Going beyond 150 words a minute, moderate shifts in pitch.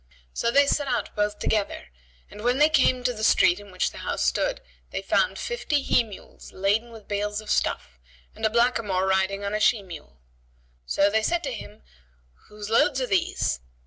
Yes: average, 195 wpm; average, 4.0 semitones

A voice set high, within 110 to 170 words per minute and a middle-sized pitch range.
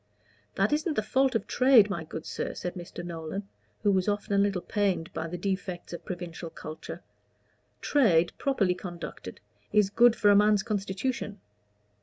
Yes: high, 200 Hz; average, 165 wpm; average, 3.5 semitones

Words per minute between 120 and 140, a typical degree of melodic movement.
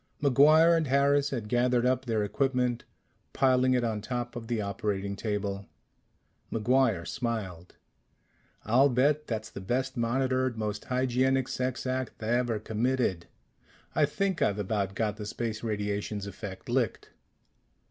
Yes: slow, 135 wpm; average, 3.6 semitones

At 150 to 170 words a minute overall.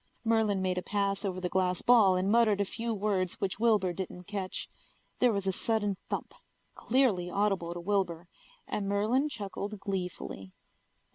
Yes: average, 160 wpm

